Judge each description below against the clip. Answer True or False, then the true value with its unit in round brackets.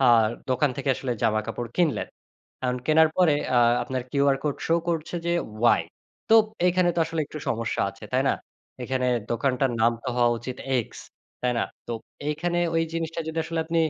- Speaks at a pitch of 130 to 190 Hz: True (140 Hz)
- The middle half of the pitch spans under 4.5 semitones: False (5.1 semitones)